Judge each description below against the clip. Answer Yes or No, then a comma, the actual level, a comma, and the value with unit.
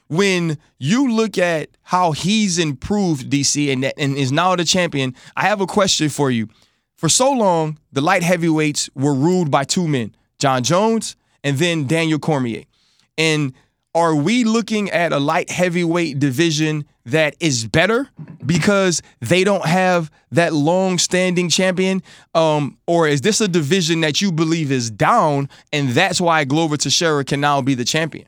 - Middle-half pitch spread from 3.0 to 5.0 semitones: Yes, average, 4.2 semitones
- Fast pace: No, average, 165 wpm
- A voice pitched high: No, medium, 160 Hz